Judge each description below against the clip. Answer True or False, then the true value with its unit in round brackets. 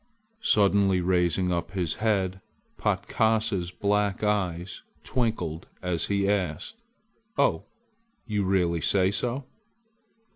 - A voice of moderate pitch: False (95 Hz)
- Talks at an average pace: False (100 wpm)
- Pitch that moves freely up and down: False (2.6 semitones)